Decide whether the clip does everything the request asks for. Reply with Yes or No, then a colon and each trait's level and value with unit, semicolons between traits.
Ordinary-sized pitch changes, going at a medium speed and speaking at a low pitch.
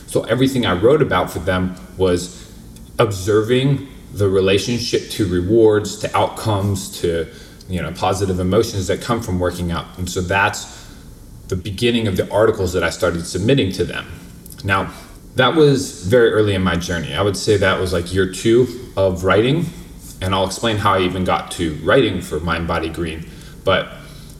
Yes: average, 3.5 semitones; average, 175 wpm; very low, 95 Hz